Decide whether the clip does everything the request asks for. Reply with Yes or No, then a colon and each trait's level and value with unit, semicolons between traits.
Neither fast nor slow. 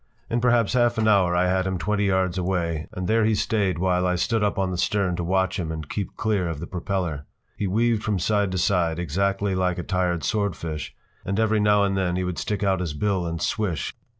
No: fast, 235 wpm